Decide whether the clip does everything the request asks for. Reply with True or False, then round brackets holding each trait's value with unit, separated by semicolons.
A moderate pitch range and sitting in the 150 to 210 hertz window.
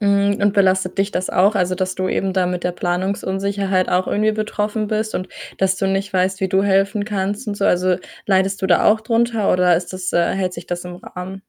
False (1.8 semitones; 190 Hz)